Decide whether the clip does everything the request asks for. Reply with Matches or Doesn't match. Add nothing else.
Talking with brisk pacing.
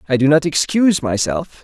Doesn't match